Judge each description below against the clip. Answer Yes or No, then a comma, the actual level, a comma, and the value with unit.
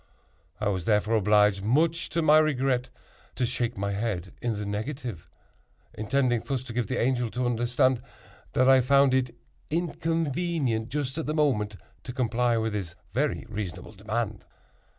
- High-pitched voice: No, low, 120 Hz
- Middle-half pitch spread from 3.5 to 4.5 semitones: Yes, average, 4.2 semitones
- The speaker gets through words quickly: No, average, 150 wpm